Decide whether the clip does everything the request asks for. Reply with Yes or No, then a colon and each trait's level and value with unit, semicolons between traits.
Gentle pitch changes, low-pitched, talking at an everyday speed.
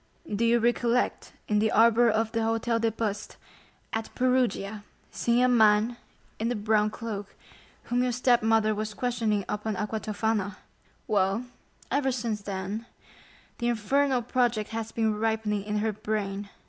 No: narrow, 2.1 semitones; high, 220 Hz; average, 145 wpm